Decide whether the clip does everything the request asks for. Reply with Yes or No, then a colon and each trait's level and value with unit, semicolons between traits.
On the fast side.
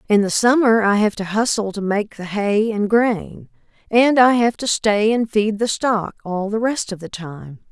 Yes: fast, 220 wpm